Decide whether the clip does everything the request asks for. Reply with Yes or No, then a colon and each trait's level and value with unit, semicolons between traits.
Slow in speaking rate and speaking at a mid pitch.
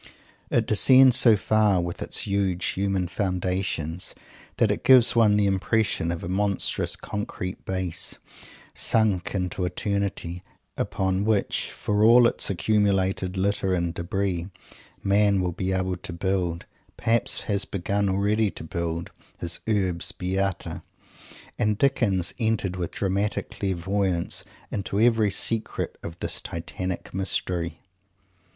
No: slow, 125 wpm; very low, 95 Hz